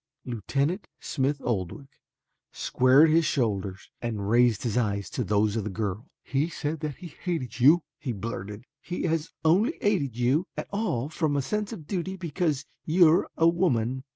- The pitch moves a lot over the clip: Yes, wide, 6.3 semitones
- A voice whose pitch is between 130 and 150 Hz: Yes, medium, 140 Hz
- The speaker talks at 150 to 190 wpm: Yes, average, 170 wpm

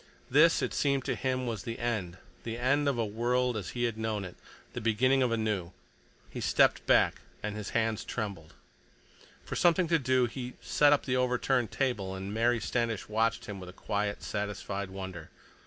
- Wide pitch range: No, average, 3.7 semitones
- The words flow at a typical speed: Yes, average, 190 wpm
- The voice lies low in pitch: Yes, low, 115 Hz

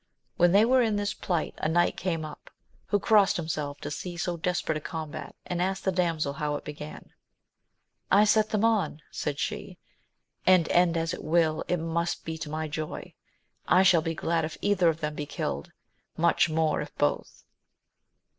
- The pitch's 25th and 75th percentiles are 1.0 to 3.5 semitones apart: Yes, average, 3.1 semitones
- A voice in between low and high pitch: Yes, medium, 165 Hz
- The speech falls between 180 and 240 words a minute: Yes, average, 185 wpm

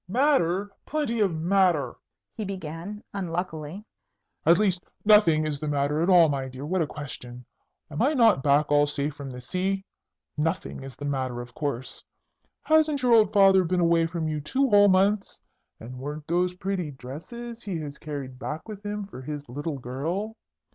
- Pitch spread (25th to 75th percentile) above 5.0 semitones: Yes, wide, 5.5 semitones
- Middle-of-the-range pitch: Yes, medium, 165 Hz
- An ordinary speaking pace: Yes, average, 175 wpm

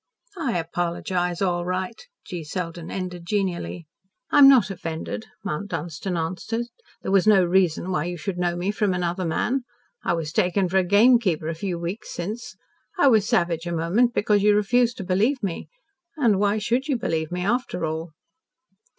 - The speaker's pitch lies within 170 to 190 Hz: Yes, medium, 185 Hz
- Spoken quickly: No, average, 175 wpm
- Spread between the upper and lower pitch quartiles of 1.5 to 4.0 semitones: Yes, average, 3.5 semitones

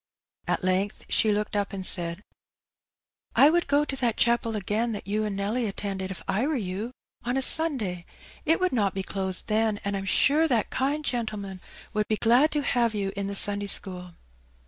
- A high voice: Yes, high, 210 Hz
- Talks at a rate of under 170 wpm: No, average, 200 wpm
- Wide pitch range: No, average, 3.9 semitones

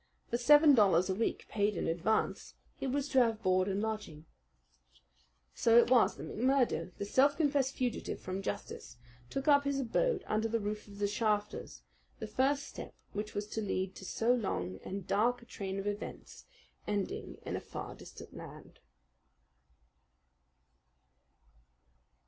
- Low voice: No, high, 215 Hz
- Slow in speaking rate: No, average, 155 wpm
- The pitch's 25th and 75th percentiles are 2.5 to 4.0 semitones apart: No, average, 4.6 semitones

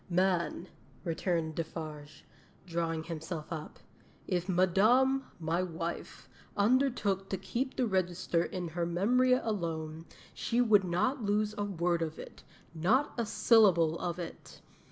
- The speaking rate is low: Yes, slow, 130 wpm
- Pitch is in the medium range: Yes, medium, 180 Hz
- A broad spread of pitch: No, average, 4.1 semitones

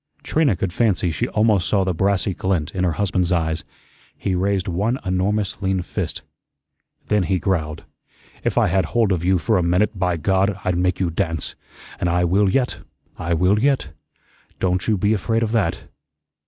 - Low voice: Yes, very low, 95 Hz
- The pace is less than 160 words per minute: No, average, 180 wpm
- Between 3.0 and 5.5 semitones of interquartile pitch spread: No, narrow, 2.6 semitones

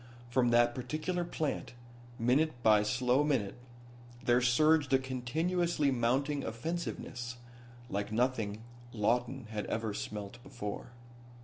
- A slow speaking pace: Yes, slow, 110 wpm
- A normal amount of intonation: Yes, average, 3.7 semitones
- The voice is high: No, low, 125 Hz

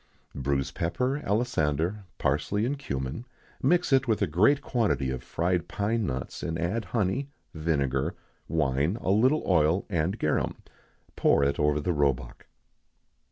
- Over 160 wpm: No, average, 145 wpm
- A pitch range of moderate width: No, wide, 7.8 semitones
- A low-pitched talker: Yes, very low, 85 Hz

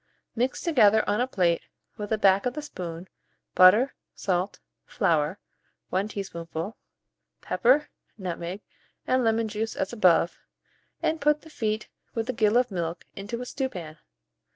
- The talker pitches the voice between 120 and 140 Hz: No, high, 210 Hz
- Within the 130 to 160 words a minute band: Yes, average, 145 wpm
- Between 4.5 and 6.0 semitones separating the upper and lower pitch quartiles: Yes, average, 5.0 semitones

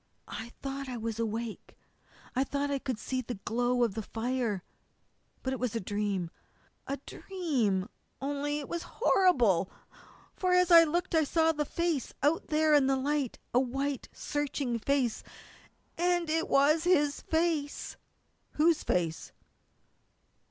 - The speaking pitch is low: No, very high, 275 Hz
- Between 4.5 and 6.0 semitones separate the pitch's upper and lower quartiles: Yes, average, 4.9 semitones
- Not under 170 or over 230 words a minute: No, average, 145 wpm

